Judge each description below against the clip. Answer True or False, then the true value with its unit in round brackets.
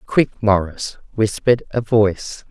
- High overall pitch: False (110 Hz)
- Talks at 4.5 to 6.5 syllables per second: False (4.3 syllables/s)